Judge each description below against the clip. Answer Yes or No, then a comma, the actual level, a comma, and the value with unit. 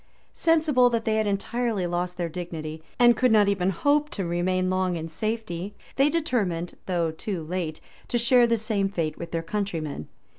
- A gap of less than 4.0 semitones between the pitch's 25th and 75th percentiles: No, average, 5.2 semitones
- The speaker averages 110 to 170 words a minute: No, average, 180 wpm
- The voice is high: Yes, high, 195 Hz